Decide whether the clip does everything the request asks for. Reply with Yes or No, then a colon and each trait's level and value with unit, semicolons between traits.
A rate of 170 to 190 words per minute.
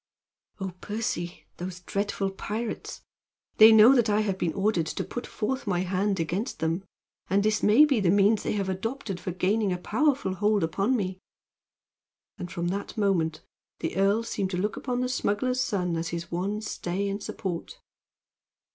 Yes: average, 175 wpm